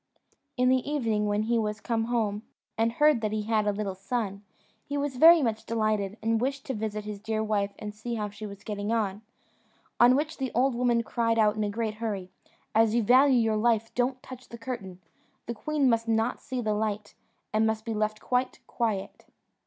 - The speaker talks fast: Yes, fast, 210 wpm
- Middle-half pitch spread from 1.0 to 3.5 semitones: Yes, narrow, 2.5 semitones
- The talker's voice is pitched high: Yes, high, 225 Hz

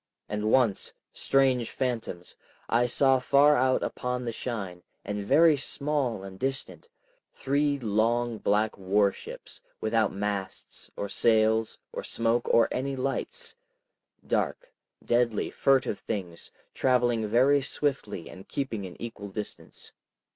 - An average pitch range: Yes, average, 4.2 semitones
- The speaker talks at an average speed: No, slow, 115 wpm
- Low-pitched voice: Yes, low, 120 Hz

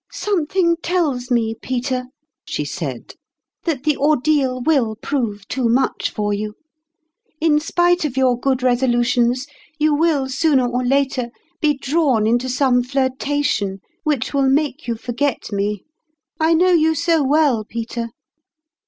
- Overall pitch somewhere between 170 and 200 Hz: No, very high, 265 Hz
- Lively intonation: No, average, 3.9 semitones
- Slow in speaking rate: No, average, 145 wpm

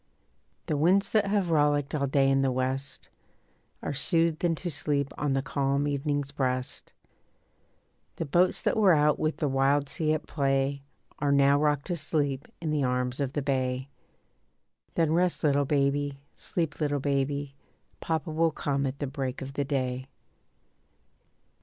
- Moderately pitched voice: Yes, medium, 145 Hz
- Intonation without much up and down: Yes, narrow, 2.2 semitones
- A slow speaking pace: No, average, 160 wpm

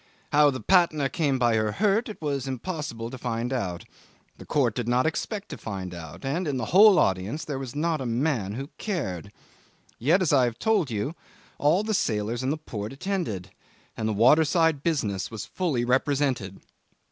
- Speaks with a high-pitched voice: No, low, 135 Hz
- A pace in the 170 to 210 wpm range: Yes, average, 180 wpm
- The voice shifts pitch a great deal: Yes, wide, 6.0 semitones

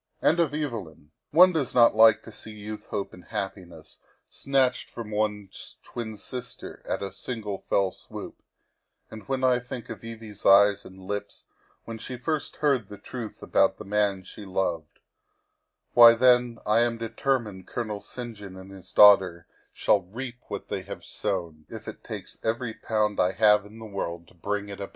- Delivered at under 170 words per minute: No, average, 180 wpm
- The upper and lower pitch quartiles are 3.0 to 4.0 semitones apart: Yes, average, 3.4 semitones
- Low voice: Yes, low, 105 Hz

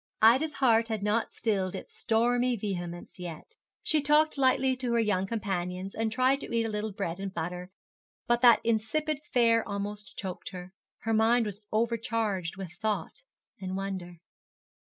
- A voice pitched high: Yes, high, 220 Hz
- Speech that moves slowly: No, average, 160 wpm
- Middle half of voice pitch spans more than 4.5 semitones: No, average, 3.7 semitones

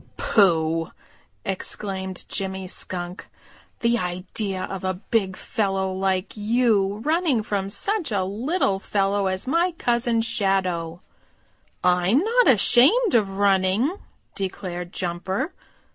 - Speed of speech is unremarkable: No, slow, 110 wpm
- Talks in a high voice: Yes, high, 195 Hz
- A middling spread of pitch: Yes, average, 3.9 semitones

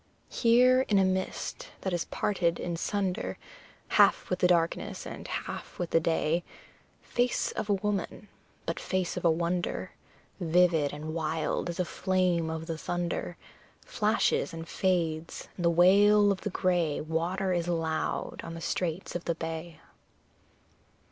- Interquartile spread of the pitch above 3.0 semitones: No, narrow, 2.4 semitones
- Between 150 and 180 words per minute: Yes, average, 155 wpm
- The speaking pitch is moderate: Yes, medium, 175 Hz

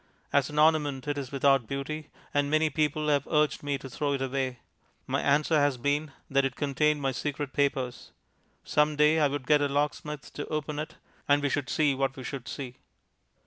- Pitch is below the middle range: No, medium, 145 Hz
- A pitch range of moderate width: No, narrow, 1.7 semitones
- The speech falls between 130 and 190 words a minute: No, average, 200 wpm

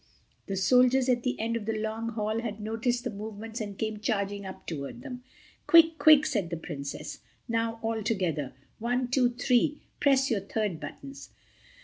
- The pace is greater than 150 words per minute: Yes, average, 160 wpm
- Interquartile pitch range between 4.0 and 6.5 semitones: No, average, 3.3 semitones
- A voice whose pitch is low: No, high, 225 Hz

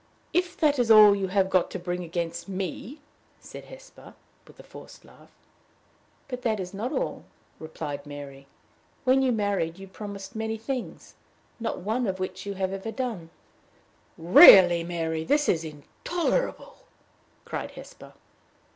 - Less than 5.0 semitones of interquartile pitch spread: No, average, 5.3 semitones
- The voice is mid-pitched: No, high, 195 Hz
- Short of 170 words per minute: Yes, average, 150 wpm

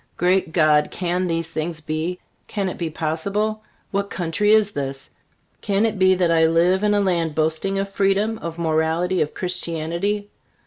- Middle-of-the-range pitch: Yes, medium, 175 Hz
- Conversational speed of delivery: Yes, average, 170 wpm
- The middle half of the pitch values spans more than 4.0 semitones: No, average, 3.5 semitones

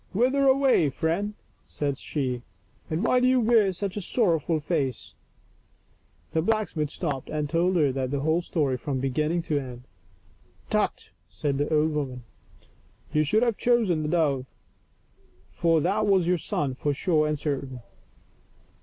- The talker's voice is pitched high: No, medium, 155 Hz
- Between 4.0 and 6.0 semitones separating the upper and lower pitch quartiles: Yes, wide, 5.4 semitones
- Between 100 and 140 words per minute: No, average, 170 wpm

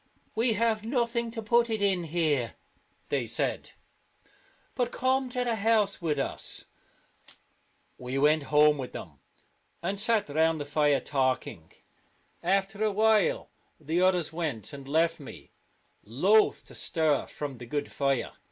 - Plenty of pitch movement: Yes, wide, 7.2 semitones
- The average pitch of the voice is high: No, medium, 165 Hz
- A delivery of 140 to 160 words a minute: Yes, average, 150 wpm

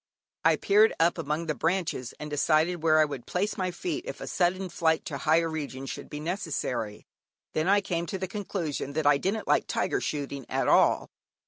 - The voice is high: No, medium, 160 Hz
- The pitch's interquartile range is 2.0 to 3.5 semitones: No, average, 4.1 semitones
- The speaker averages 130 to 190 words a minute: No, average, 200 wpm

